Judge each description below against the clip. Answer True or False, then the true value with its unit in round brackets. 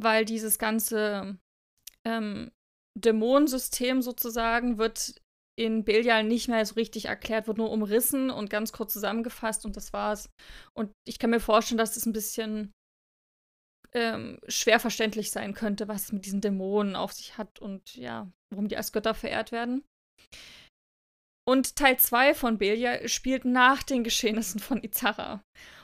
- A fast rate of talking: False (155 wpm)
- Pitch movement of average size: False (1.9 semitones)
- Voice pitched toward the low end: False (225 Hz)